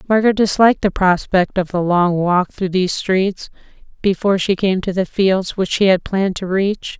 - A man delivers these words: No, female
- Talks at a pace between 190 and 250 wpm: Yes, average, 195 wpm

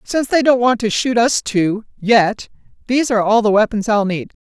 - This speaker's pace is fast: No, average, 190 wpm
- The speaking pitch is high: Yes, high, 225 Hz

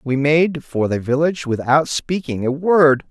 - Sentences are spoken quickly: No, average, 175 wpm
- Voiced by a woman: No, male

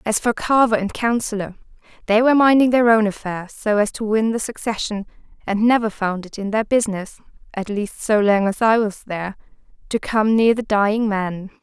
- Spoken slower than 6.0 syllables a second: Yes, 4.7 syllables/s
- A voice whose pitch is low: No, high, 215 Hz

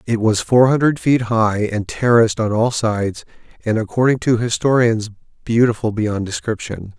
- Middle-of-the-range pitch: No, low, 115 Hz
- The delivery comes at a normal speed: Yes, average, 155 wpm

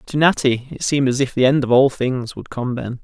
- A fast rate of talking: Yes, fast, 275 wpm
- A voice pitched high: No, low, 130 Hz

